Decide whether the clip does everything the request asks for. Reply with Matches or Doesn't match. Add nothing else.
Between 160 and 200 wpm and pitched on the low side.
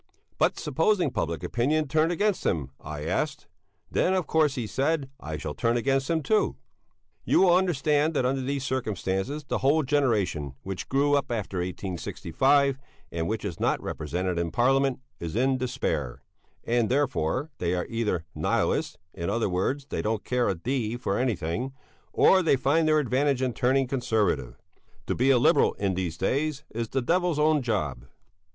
Matches